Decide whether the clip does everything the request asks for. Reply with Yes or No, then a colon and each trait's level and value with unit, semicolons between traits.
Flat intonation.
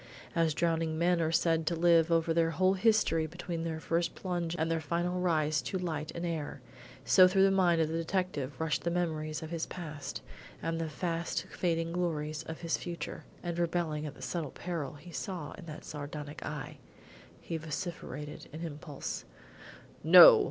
Yes: narrow, 2.0 semitones